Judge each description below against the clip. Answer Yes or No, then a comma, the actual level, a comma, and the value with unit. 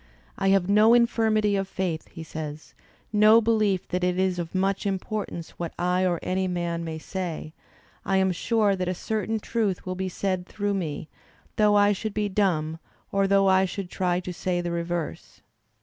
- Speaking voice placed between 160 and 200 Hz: Yes, high, 190 Hz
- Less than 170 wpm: No, average, 185 wpm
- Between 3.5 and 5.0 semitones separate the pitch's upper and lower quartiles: No, narrow, 2.6 semitones